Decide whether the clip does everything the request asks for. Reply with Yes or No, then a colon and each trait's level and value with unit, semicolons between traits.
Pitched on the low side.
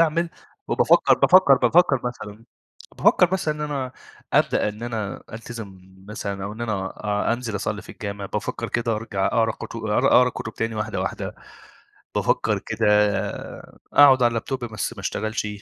Yes: low, 115 Hz